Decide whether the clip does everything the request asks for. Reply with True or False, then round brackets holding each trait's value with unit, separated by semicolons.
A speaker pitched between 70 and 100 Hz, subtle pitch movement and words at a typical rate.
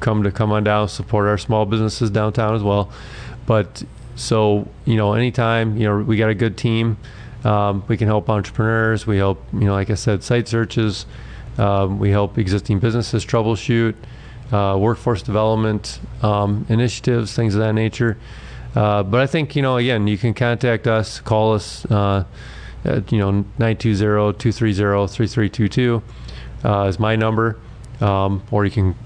False (110 Hz; 1.9 semitones; 165 wpm)